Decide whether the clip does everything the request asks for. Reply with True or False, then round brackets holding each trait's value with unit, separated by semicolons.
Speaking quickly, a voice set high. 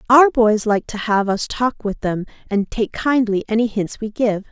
True (215 wpm; 220 Hz)